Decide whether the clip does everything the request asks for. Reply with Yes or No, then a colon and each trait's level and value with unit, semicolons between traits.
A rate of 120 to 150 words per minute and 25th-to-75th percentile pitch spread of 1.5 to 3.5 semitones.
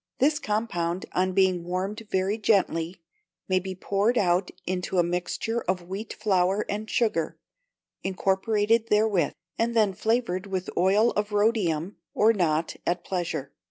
Yes: average, 140 wpm; average, 3.1 semitones